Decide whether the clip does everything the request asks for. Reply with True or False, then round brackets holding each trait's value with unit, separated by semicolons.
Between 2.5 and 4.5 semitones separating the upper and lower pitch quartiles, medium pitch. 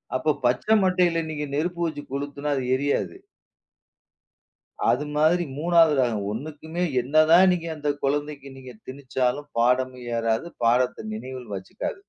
True (3.7 semitones; 145 Hz)